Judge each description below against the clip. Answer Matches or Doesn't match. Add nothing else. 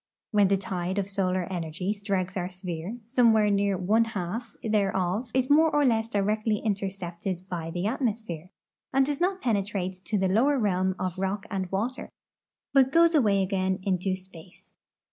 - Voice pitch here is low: Doesn't match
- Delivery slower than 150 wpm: Doesn't match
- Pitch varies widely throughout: Doesn't match